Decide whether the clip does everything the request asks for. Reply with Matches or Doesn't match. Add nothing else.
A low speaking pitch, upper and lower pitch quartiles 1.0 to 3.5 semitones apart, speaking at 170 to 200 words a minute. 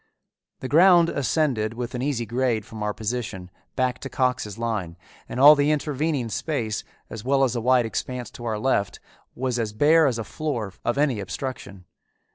Doesn't match